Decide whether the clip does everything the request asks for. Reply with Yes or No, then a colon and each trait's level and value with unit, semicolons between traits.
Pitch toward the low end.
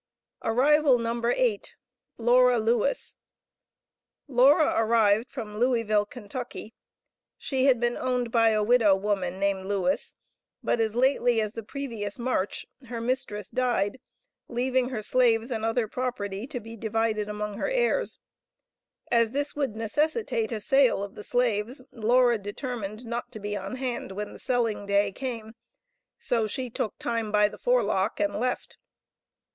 No: high, 230 Hz